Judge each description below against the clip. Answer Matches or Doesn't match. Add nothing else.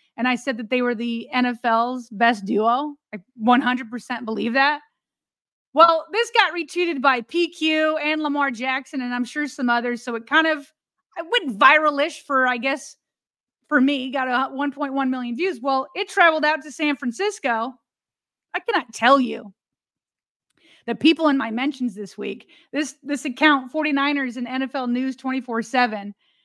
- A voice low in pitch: Doesn't match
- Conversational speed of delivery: Matches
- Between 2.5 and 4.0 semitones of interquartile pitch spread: Matches